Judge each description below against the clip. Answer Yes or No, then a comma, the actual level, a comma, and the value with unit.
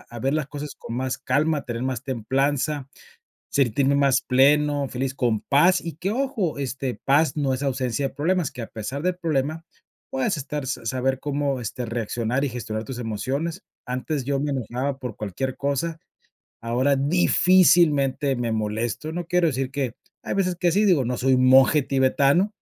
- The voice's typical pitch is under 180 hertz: Yes, low, 135 Hz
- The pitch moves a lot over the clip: No, average, 3.2 semitones